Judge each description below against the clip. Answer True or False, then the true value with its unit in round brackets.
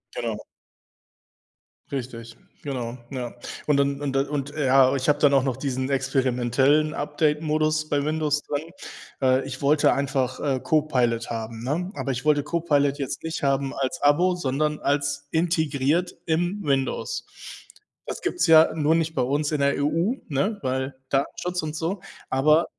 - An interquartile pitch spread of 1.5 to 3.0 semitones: True (2.6 semitones)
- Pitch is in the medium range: True (145 Hz)